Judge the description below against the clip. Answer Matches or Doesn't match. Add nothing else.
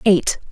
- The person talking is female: Matches